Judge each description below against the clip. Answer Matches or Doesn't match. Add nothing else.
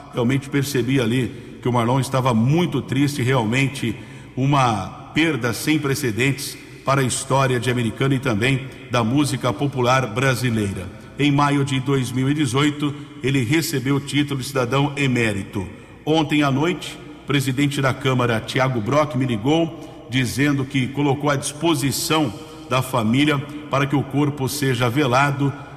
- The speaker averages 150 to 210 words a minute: Doesn't match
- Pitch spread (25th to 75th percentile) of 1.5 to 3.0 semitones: Matches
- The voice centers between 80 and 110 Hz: Doesn't match